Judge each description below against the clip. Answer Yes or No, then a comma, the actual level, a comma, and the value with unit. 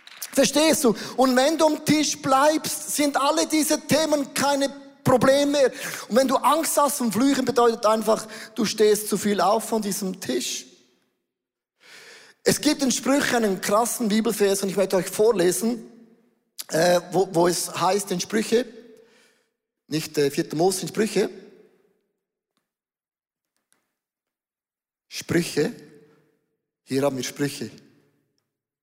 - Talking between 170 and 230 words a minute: No, slow, 125 wpm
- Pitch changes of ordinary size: No, wide, 7.1 semitones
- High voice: Yes, high, 220 Hz